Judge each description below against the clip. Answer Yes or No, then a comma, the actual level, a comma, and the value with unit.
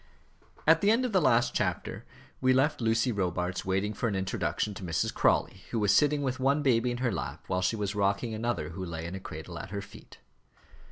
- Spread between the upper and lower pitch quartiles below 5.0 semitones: No, average, 5.3 semitones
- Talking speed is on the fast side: Yes, fast, 220 wpm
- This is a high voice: No, low, 110 Hz